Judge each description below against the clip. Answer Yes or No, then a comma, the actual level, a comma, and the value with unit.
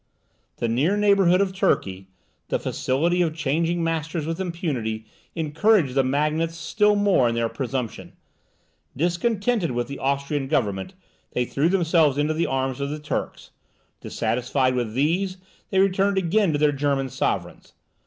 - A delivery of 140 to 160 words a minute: Yes, average, 145 wpm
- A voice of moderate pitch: Yes, medium, 155 Hz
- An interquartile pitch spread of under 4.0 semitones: No, average, 5.1 semitones